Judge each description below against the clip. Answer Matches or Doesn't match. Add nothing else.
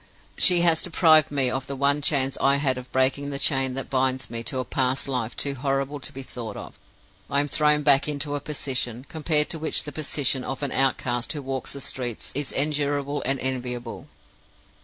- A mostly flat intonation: Matches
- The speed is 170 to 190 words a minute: Doesn't match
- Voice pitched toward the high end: Doesn't match